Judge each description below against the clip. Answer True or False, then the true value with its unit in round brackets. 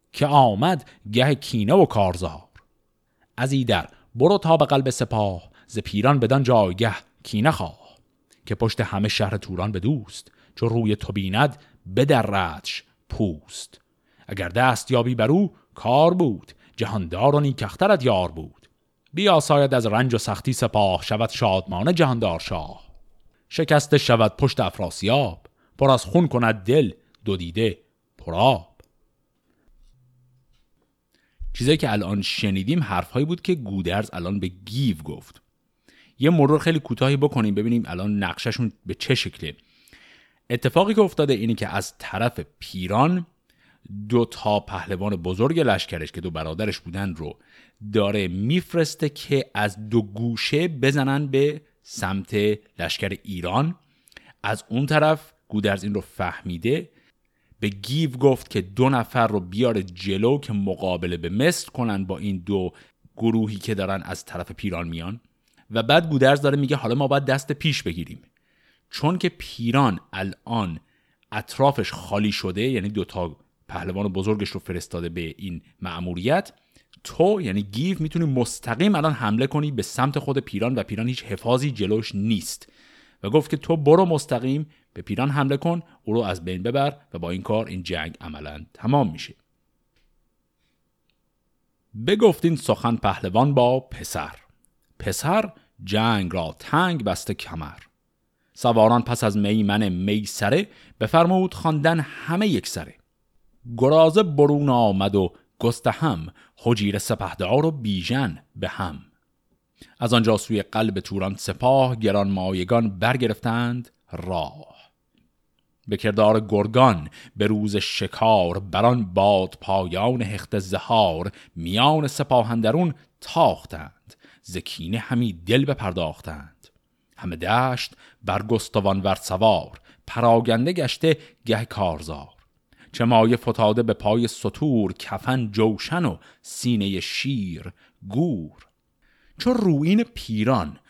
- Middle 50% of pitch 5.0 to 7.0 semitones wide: True (5.5 semitones)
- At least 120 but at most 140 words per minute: True (130 wpm)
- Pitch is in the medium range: False (115 Hz)